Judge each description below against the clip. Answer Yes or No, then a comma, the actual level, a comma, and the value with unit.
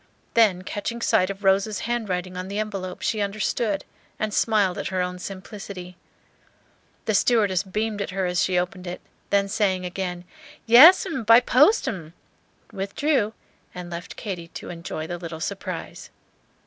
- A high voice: Yes, high, 195 Hz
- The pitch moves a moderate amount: Yes, average, 3.0 semitones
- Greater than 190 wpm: No, average, 155 wpm